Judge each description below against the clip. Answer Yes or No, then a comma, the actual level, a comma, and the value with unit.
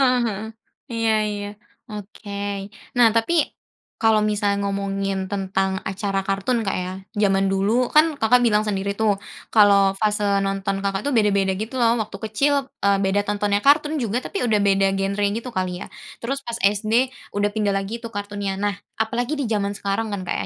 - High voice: Yes, high, 205 Hz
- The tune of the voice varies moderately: No, narrow, 2.1 semitones